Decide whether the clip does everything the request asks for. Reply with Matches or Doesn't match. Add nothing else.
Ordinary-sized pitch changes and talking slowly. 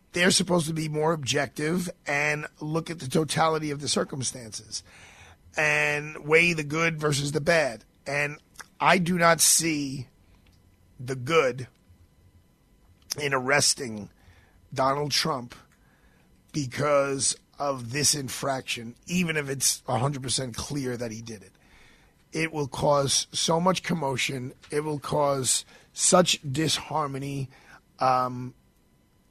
Matches